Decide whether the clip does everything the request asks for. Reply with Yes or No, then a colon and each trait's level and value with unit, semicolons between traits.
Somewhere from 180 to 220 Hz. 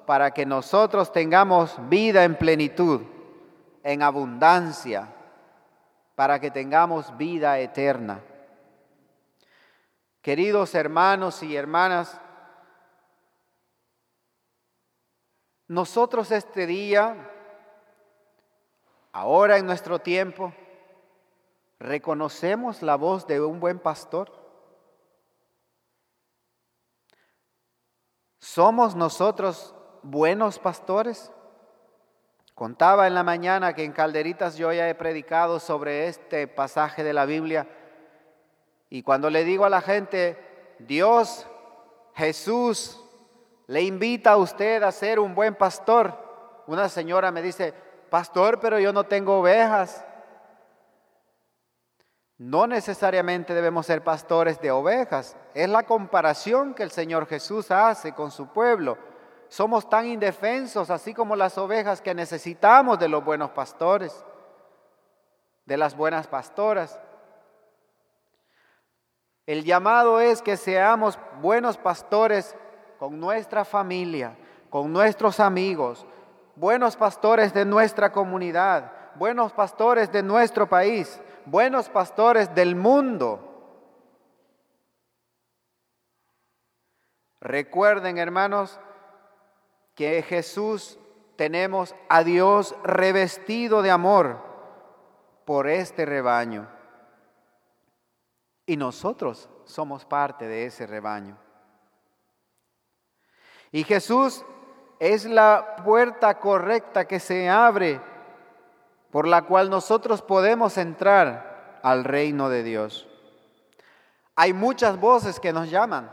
Yes: medium, 185 Hz